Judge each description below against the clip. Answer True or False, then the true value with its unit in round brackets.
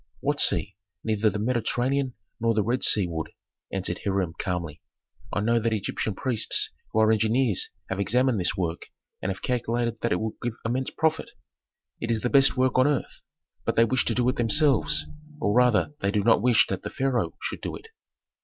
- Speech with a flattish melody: False (3.7 semitones)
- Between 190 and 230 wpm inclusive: True (195 wpm)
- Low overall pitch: True (115 Hz)